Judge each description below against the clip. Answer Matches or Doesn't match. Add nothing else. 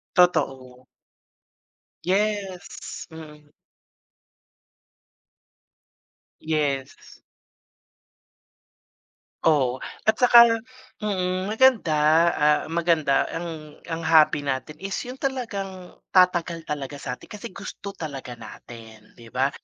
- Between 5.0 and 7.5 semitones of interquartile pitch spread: Matches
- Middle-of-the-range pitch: Matches